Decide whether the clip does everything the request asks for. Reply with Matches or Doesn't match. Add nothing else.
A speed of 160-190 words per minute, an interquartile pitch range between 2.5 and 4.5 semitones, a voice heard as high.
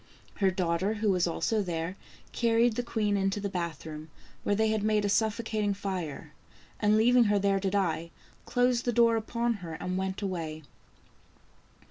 Matches